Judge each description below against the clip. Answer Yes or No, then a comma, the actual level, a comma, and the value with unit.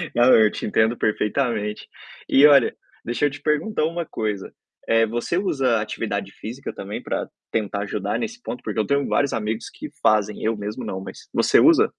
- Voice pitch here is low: Yes, low, 115 Hz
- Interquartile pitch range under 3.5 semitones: No, average, 4.7 semitones